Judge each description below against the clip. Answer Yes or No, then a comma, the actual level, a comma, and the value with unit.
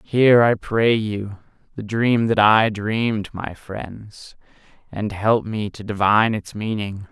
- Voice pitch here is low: Yes, low, 105 Hz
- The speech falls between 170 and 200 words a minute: No, average, 150 wpm